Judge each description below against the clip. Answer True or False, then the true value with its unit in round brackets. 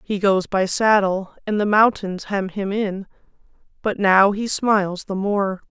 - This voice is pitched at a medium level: False (200 Hz)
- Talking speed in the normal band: True (170 wpm)